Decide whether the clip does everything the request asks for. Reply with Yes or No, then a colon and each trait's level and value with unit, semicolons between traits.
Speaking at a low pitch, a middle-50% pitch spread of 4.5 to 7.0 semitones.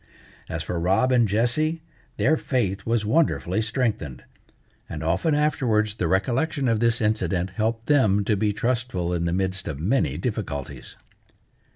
Yes: low, 110 Hz; average, 5.1 semitones